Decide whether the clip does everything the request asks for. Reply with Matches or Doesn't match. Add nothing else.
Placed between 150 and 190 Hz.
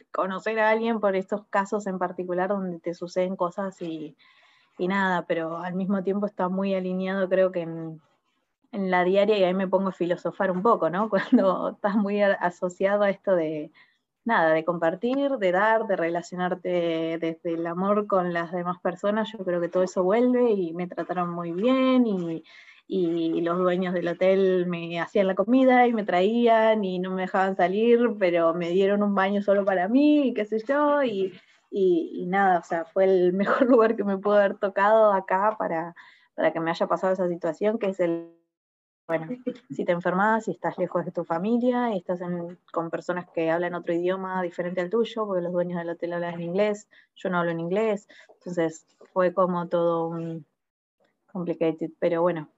Matches